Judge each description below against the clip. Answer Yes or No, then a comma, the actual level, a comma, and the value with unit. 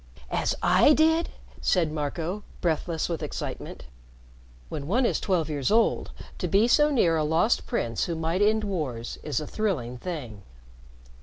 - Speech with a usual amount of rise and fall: No, wide, 6.1 semitones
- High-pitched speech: No, medium, 170 Hz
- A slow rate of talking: No, average, 155 wpm